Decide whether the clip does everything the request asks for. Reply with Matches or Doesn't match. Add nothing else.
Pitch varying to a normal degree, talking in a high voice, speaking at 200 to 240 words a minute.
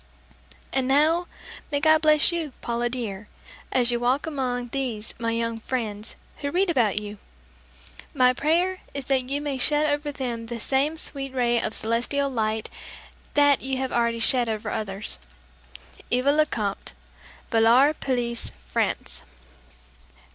Doesn't match